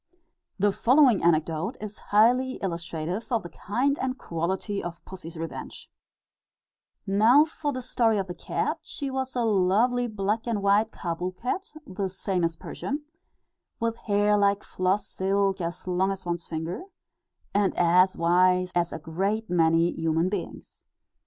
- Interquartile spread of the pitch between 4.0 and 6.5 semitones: Yes, average, 4.4 semitones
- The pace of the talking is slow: No, average, 150 wpm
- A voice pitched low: No, high, 195 Hz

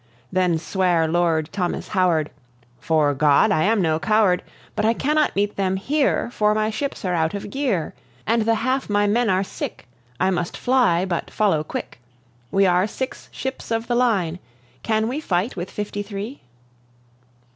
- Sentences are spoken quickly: No, average, 170 wpm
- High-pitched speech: Yes, high, 200 Hz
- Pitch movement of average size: Yes, average, 4.4 semitones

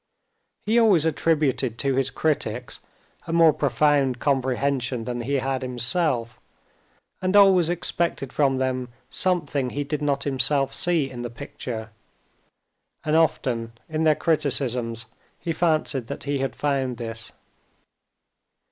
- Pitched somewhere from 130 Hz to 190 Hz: Yes, low, 135 Hz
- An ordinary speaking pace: No, slow, 130 wpm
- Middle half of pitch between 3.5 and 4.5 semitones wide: Yes, average, 3.9 semitones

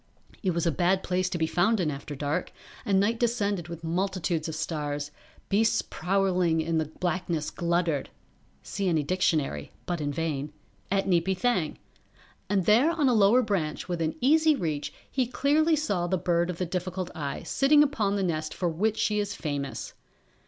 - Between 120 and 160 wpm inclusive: No, average, 175 wpm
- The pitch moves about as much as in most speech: Yes, average, 4.2 semitones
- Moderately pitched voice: Yes, medium, 180 Hz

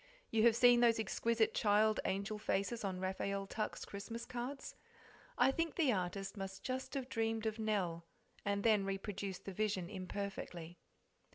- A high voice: Yes, high, 210 Hz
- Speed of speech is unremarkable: Yes, average, 155 wpm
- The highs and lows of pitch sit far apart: No, average, 2.9 semitones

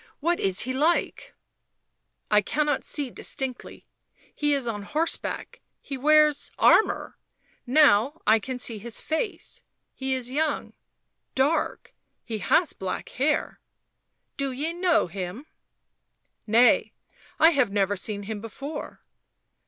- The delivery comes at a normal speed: Yes, average, 145 wpm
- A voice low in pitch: No, very high, 265 Hz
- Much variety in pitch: Yes, wide, 5.7 semitones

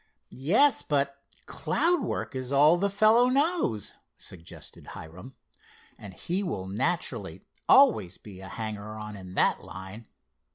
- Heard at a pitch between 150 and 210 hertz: No, low, 125 Hz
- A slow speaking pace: Yes, slow, 130 wpm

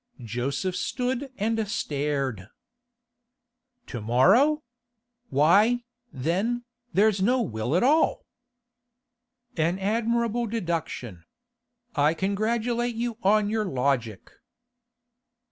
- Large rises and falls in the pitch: Yes, wide, 8.7 semitones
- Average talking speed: No, slow, 85 wpm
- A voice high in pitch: Yes, high, 195 Hz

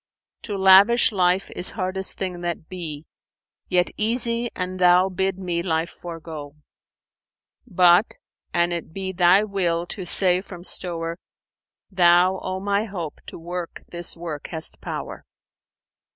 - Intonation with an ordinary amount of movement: No, narrow, 1.9 semitones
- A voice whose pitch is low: No, medium, 180 Hz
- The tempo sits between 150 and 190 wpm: No, average, 140 wpm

